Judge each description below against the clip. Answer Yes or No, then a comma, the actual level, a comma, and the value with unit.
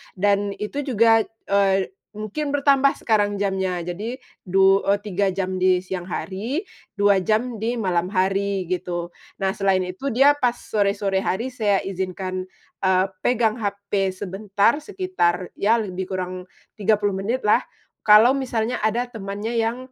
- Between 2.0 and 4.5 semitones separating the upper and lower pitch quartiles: Yes, average, 3.1 semitones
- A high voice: Yes, high, 200 Hz